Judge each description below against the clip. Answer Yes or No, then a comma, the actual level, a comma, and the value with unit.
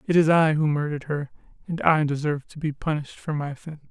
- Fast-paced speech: Yes, fast, 230 wpm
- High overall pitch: No, medium, 150 Hz